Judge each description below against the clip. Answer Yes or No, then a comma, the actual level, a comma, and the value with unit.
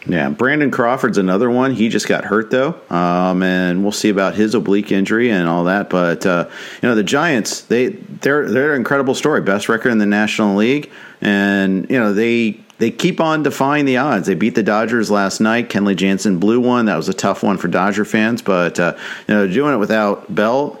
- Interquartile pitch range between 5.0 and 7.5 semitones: No, average, 3.2 semitones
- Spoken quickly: Yes, fast, 215 wpm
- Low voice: Yes, low, 105 Hz